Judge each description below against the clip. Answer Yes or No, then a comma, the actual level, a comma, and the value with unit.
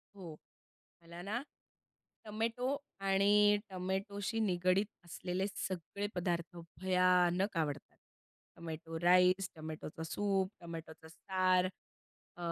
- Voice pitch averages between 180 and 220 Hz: Yes, medium, 185 Hz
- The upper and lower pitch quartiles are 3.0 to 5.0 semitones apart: No, narrow, 2.6 semitones